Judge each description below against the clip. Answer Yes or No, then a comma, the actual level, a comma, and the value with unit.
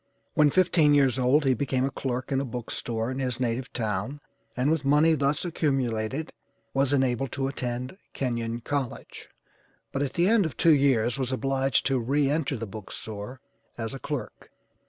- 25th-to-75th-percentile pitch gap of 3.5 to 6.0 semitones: No, average, 2.8 semitones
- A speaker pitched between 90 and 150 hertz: Yes, low, 135 Hz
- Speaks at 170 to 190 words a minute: Yes, average, 180 wpm